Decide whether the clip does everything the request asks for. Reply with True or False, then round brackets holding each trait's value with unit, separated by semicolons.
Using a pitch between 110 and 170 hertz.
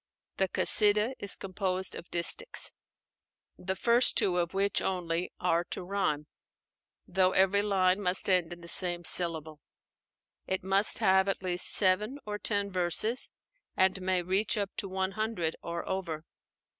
False (190 Hz)